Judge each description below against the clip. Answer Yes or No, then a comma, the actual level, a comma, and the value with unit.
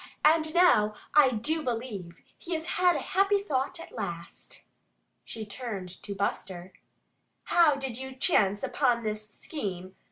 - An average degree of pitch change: No, wide, 7.5 semitones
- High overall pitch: Yes, very high, 250 Hz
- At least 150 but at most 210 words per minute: No, average, 140 wpm